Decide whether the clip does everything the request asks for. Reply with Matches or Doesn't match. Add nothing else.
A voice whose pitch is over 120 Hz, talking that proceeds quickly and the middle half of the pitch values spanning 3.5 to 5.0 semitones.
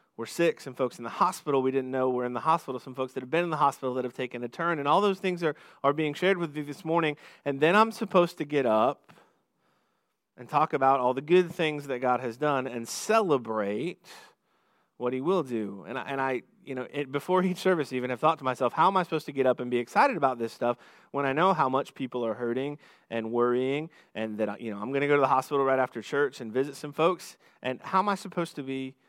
Matches